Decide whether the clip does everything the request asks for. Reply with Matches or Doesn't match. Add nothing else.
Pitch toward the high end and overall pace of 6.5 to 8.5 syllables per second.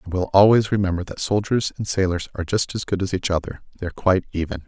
Doesn't match